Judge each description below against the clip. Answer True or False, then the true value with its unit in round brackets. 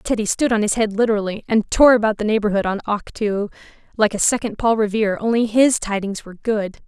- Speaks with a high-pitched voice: True (215 Hz)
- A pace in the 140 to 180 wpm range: False (190 wpm)